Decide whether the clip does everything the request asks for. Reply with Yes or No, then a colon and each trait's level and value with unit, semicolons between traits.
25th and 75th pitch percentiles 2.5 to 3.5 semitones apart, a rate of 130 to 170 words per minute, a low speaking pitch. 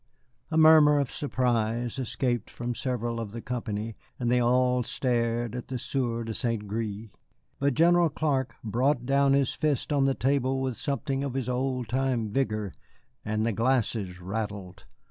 Yes: average, 2.9 semitones; average, 165 wpm; low, 125 Hz